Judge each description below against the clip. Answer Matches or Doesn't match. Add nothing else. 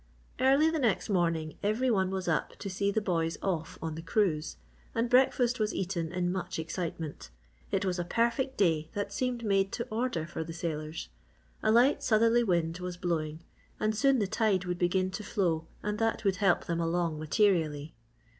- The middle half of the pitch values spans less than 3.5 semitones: Doesn't match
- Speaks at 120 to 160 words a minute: Doesn't match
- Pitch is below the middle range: Doesn't match